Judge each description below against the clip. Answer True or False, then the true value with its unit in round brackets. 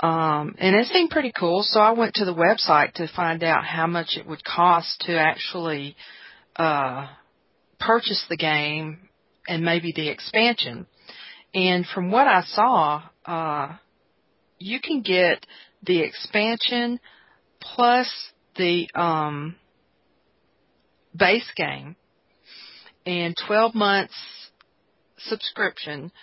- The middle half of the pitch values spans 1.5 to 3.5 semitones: False (5.0 semitones)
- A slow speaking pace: True (115 wpm)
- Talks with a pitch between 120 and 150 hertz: False (175 Hz)